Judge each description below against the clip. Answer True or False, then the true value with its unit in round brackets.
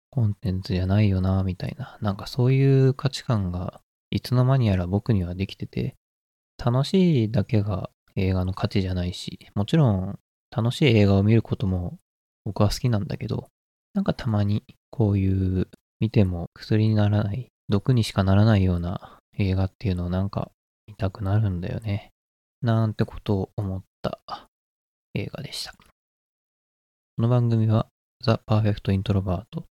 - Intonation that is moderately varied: True (3.5 semitones)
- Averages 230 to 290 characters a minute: False (330 characters per minute)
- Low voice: True (105 Hz)